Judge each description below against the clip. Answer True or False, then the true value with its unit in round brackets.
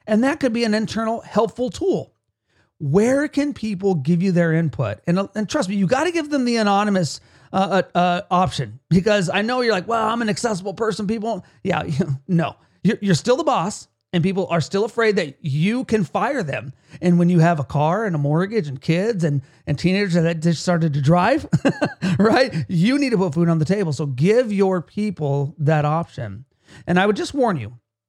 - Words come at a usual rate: False (210 wpm)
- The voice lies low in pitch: False (185 Hz)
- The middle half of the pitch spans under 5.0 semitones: False (5.6 semitones)